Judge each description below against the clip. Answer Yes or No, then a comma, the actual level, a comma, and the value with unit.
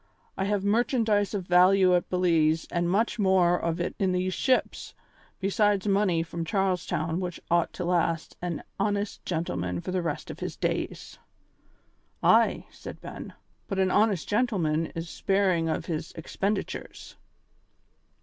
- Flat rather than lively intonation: No, average, 3.0 semitones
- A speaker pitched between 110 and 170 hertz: No, medium, 180 Hz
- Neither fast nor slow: Yes, average, 150 wpm